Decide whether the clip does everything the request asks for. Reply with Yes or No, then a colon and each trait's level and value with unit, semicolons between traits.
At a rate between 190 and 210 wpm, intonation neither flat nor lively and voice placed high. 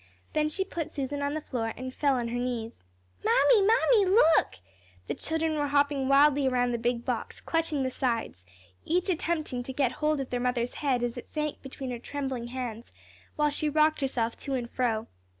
Yes: average, 195 wpm; average, 3.7 semitones; very high, 270 Hz